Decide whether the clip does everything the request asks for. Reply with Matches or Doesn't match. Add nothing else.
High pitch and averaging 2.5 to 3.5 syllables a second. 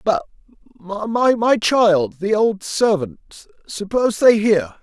Matches